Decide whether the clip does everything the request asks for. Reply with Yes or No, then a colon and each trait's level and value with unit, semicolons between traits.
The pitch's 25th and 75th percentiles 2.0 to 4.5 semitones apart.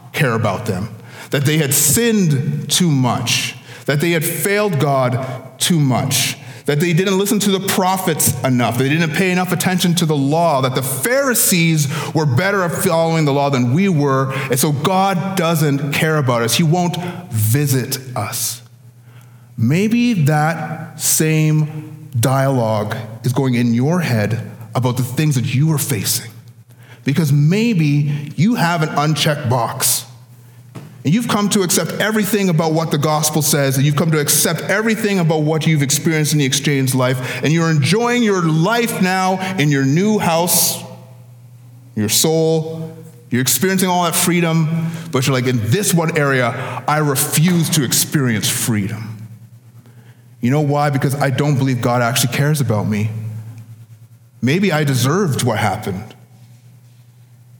No: average, 5.1 semitones